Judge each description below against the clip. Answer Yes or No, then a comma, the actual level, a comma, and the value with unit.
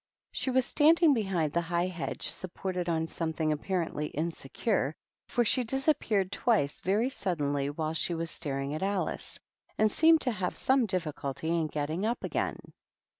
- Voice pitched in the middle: Yes, medium, 180 Hz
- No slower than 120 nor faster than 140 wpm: No, average, 160 wpm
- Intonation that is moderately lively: No, wide, 6.1 semitones